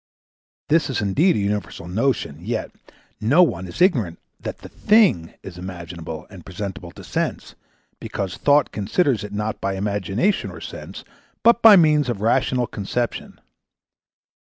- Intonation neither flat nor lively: No, wide, 7.2 semitones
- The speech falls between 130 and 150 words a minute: Yes, average, 145 wpm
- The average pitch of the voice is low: Yes, low, 105 Hz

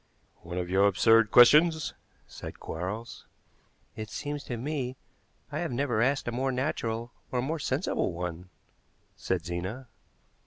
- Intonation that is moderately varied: No, wide, 6.0 semitones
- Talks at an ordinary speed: Yes, average, 145 wpm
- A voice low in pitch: Yes, low, 120 Hz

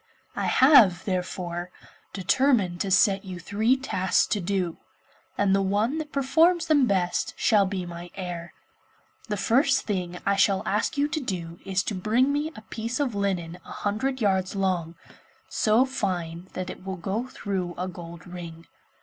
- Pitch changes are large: No, average, 4.8 semitones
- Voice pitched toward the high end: Yes, high, 195 Hz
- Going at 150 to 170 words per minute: Yes, average, 165 wpm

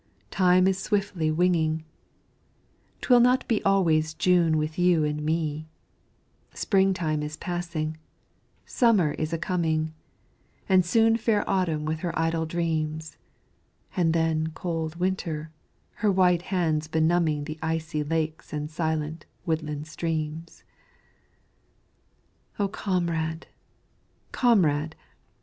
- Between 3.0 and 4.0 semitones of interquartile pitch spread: No, narrow, 2.5 semitones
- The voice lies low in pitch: No, medium, 165 Hz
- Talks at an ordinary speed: No, slow, 110 wpm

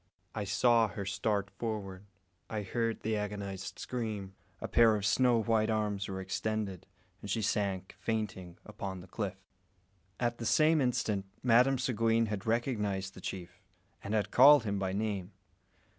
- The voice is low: Yes, low, 105 Hz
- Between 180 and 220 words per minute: No, average, 155 wpm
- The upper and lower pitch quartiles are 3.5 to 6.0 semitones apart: No, average, 2.8 semitones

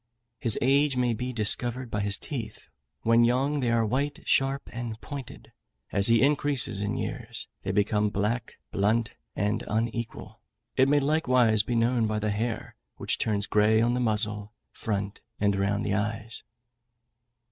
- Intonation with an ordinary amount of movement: Yes, average, 3.0 semitones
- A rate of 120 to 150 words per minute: No, average, 160 wpm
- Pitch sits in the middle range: No, low, 115 Hz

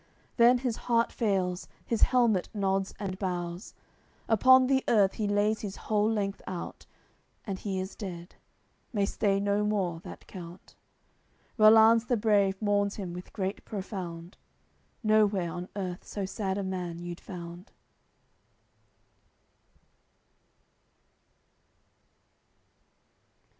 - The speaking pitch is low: No, high, 200 Hz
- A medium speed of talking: No, slow, 115 wpm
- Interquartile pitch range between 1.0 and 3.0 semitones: Yes, average, 2.7 semitones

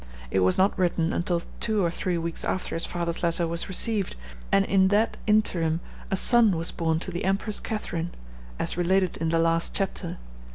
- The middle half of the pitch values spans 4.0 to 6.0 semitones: No, average, 2.8 semitones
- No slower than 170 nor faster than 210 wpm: Yes, average, 190 wpm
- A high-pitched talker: No, medium, 175 Hz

